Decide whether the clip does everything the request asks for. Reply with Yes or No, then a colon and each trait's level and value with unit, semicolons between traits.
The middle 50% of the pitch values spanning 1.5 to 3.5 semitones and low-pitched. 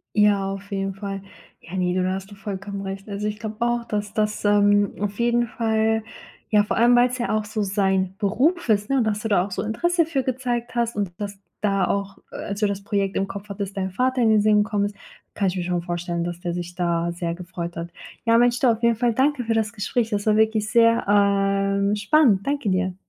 No: average, 2.7 semitones; high, 205 Hz